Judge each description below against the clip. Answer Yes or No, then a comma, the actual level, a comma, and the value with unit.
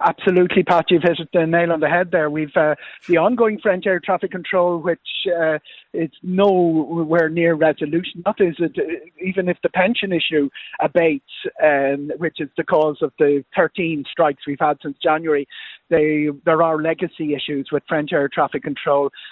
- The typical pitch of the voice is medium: Yes, medium, 165 Hz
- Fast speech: No, average, 175 wpm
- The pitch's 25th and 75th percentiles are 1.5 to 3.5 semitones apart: Yes, average, 2.9 semitones